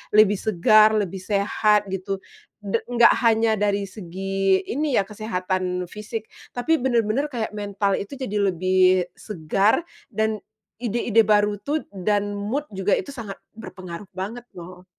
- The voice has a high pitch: Yes, high, 205 Hz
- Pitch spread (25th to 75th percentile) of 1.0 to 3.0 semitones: Yes, average, 2.7 semitones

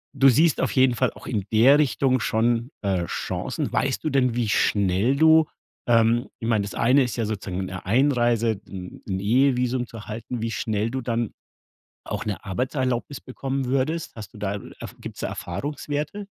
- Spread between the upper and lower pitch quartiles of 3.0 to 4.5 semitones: Yes, average, 3.9 semitones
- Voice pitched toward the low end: Yes, low, 120 Hz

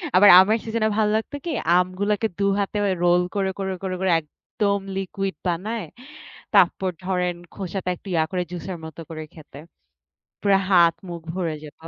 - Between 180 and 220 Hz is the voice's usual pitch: Yes, high, 190 Hz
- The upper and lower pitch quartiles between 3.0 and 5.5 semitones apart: No, narrow, 2.5 semitones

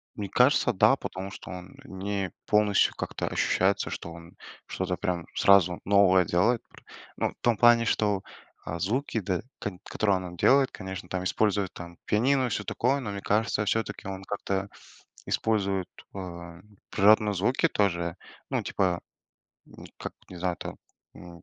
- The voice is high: No, low, 100 Hz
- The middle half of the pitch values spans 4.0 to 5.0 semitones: No, average, 2.8 semitones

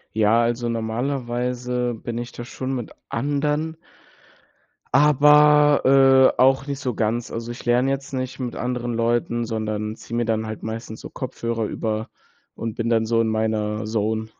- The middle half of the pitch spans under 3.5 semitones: Yes, average, 2.9 semitones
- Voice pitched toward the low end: Yes, low, 120 Hz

